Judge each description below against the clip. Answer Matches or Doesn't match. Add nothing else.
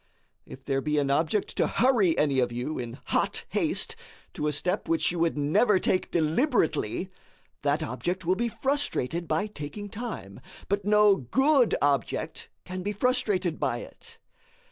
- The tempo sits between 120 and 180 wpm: Matches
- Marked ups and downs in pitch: Matches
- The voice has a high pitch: Doesn't match